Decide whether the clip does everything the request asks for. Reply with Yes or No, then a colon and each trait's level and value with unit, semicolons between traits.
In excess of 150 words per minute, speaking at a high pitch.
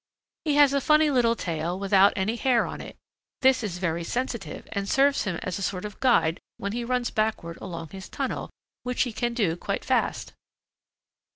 Yes: average, 190 wpm; high, 215 Hz